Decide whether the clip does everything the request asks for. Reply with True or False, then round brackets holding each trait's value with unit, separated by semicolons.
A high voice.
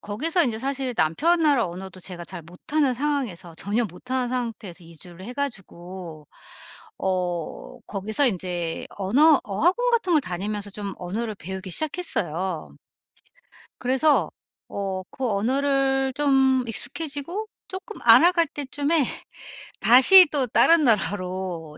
True (230 Hz)